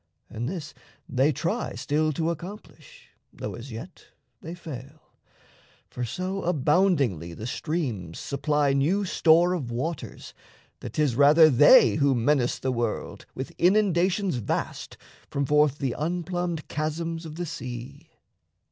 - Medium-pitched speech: Yes, medium, 150 Hz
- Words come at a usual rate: No, slow, 130 wpm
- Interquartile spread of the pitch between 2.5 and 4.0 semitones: No, average, 4.9 semitones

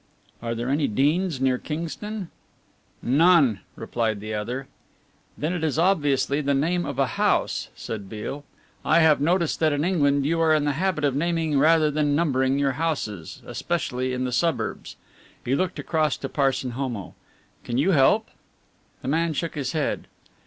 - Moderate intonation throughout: Yes, average, 4.1 semitones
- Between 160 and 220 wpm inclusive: Yes, average, 165 wpm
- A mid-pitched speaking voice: Yes, medium, 145 Hz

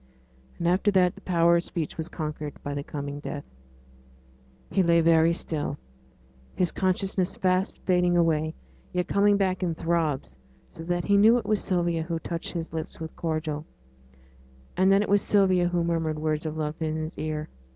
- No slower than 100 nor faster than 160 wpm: No, average, 180 wpm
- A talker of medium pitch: Yes, medium, 170 Hz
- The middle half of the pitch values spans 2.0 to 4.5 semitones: Yes, average, 2.7 semitones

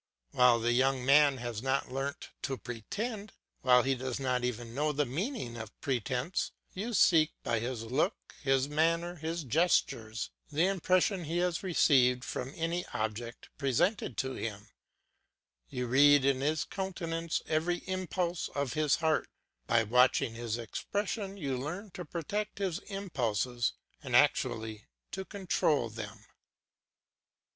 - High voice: No, medium, 140 Hz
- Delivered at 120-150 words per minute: Yes, average, 140 wpm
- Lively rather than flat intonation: Yes, wide, 6.0 semitones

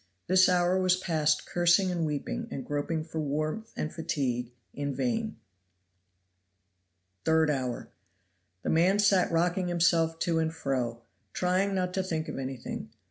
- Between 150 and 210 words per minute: No, average, 140 wpm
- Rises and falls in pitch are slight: No, average, 3.7 semitones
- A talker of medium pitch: Yes, medium, 165 Hz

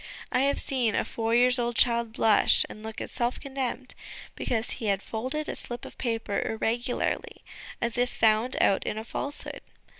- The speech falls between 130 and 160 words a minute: No, average, 180 wpm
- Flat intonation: Yes, narrow, 2.2 semitones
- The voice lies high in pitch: Yes, high, 235 Hz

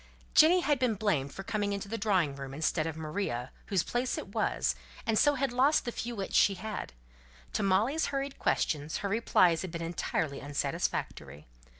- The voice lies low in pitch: No, high, 200 Hz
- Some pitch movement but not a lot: No, wide, 7.3 semitones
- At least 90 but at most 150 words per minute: No, average, 185 wpm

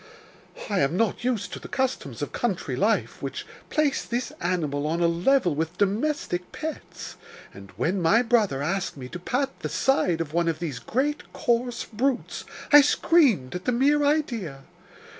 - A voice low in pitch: No, high, 205 Hz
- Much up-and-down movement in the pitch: Yes, wide, 8.0 semitones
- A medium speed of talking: Yes, average, 170 wpm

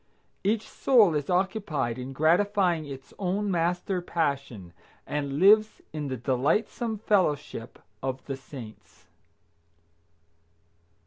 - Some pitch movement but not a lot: No, wide, 6.6 semitones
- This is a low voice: No, medium, 160 Hz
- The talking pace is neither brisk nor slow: No, slow, 105 wpm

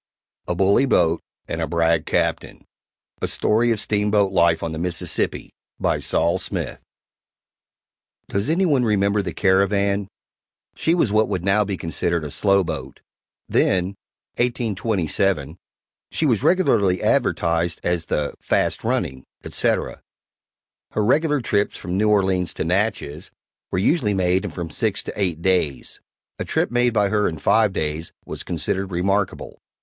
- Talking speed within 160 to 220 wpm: No, average, 145 wpm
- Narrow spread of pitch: No, average, 3.7 semitones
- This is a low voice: Yes, very low, 95 Hz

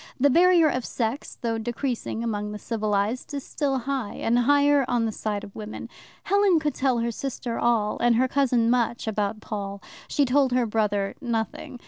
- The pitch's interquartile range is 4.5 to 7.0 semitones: No, average, 3.8 semitones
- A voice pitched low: No, high, 240 Hz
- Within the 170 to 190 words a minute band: Yes, average, 180 wpm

